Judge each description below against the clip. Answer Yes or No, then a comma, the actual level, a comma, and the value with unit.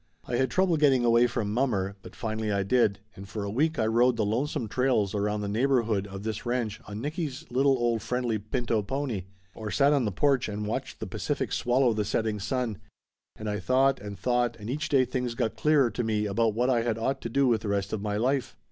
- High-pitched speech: No, low, 115 Hz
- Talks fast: Yes, fast, 230 wpm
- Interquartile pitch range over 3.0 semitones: Yes, average, 3.6 semitones